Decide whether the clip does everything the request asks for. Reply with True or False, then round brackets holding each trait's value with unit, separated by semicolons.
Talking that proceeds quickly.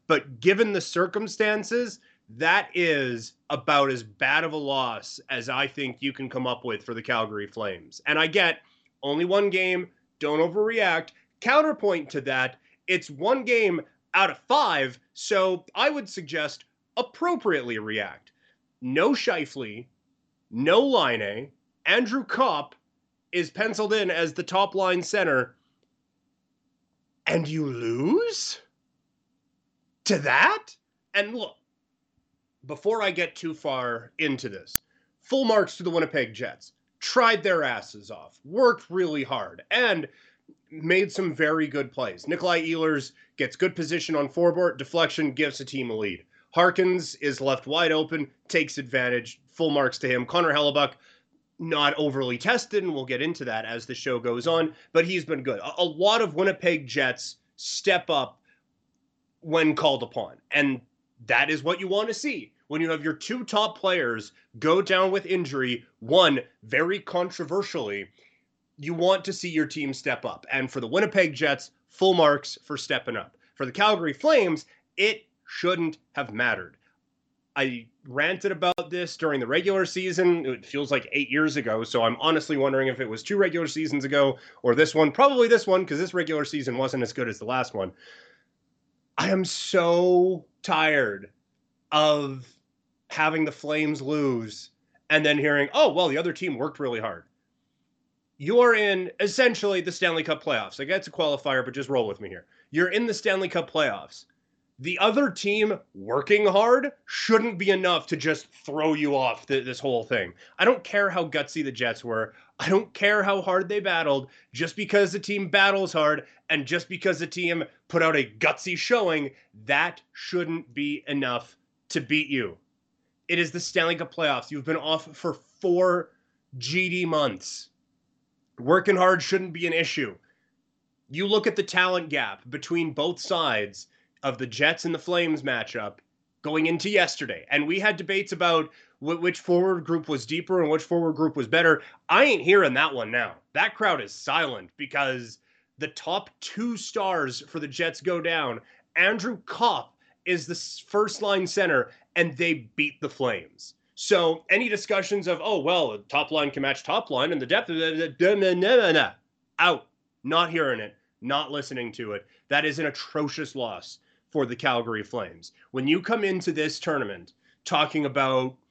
False (170 wpm)